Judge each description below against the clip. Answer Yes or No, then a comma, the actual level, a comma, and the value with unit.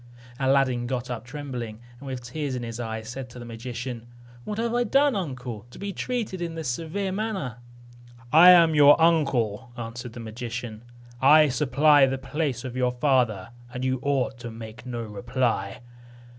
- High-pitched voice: No, low, 130 Hz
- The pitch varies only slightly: No, average, 4.3 semitones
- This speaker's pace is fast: No, average, 170 wpm